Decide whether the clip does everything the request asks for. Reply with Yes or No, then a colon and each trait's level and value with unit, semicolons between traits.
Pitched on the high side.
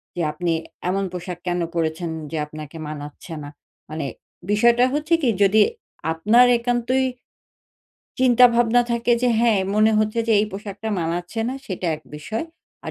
Yes: high, 210 Hz